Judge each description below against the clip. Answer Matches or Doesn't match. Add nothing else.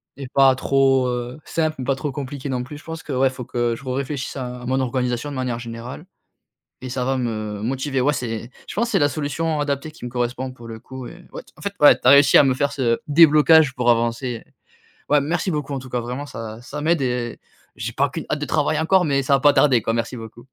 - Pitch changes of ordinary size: Matches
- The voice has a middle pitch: Doesn't match